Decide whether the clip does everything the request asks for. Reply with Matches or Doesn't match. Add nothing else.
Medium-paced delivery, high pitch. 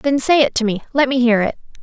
Doesn't match